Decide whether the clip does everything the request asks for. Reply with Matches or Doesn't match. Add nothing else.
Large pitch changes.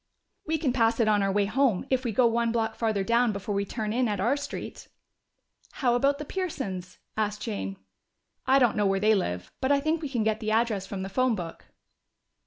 Doesn't match